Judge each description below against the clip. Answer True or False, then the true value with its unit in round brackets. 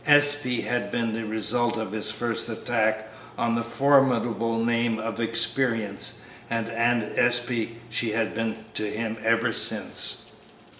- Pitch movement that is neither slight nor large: False (1.3 semitones)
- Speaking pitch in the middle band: False (115 Hz)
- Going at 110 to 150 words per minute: True (140 wpm)